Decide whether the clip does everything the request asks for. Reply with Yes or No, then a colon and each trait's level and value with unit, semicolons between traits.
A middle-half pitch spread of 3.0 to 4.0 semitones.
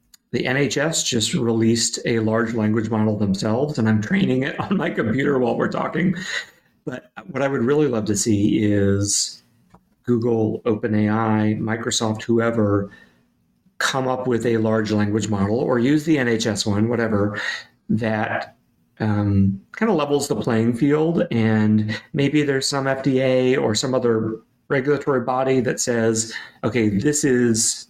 Yes: average, 3.7 semitones